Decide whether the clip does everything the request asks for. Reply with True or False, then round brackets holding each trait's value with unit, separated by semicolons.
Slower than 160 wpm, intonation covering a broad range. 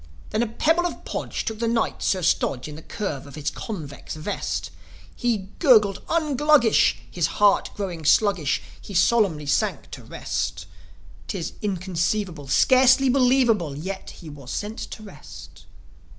True (150 wpm; 6.9 semitones)